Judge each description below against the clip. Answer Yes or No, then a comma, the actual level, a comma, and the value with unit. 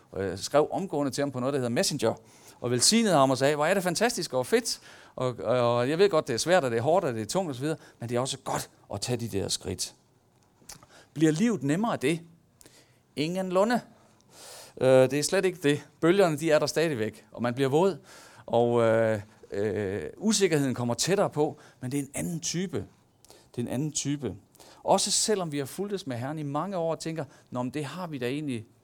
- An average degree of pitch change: No, wide, 5.7 semitones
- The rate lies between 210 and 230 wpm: Yes, fast, 225 wpm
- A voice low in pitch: No, medium, 145 Hz